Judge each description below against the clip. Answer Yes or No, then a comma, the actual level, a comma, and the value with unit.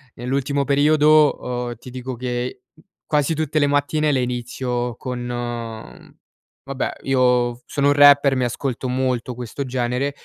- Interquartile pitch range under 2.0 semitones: No, narrow, 2.6 semitones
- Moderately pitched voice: No, low, 130 Hz